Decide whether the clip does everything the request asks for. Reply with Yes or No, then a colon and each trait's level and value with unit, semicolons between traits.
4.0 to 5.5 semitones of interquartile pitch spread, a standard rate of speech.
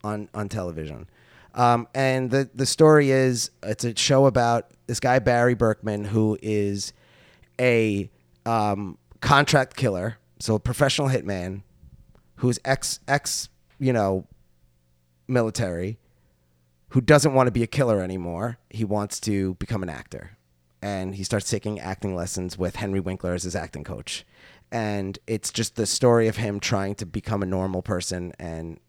Yes: average, 4.8 semitones; average, 155 wpm